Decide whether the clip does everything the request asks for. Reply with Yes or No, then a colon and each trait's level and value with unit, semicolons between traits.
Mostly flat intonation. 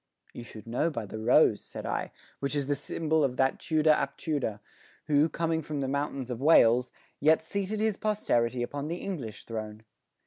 No: average, 4.8 semitones